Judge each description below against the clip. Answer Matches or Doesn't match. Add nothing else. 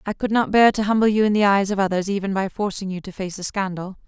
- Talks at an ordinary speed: Doesn't match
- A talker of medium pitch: Doesn't match